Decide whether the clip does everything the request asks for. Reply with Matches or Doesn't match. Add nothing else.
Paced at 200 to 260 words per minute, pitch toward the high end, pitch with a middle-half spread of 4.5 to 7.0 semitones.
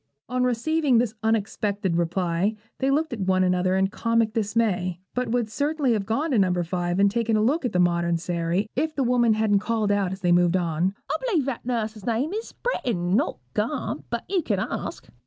Matches